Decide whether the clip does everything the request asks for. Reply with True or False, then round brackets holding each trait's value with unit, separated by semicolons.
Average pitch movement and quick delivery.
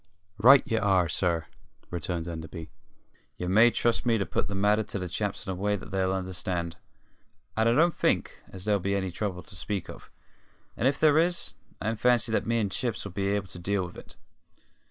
True (3.8 semitones; 210 wpm)